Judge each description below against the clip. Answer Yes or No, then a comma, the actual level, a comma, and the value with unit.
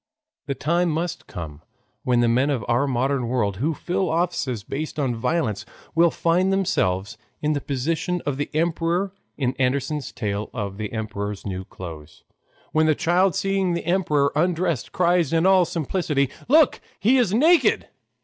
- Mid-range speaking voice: Yes, medium, 150 Hz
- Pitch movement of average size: No, wide, 6.6 semitones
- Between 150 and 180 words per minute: Yes, average, 160 wpm